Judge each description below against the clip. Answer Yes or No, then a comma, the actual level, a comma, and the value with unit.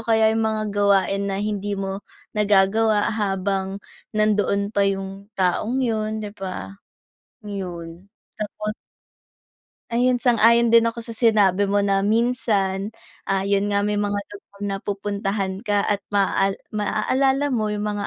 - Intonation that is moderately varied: No, narrow, 1.8 semitones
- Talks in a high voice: Yes, high, 205 Hz